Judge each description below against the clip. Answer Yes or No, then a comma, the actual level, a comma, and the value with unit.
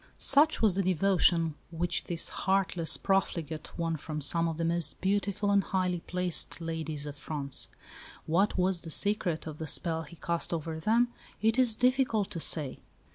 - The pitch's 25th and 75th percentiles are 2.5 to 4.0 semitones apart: Yes, average, 3.5 semitones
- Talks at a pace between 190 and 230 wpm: No, average, 170 wpm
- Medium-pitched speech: Yes, medium, 170 Hz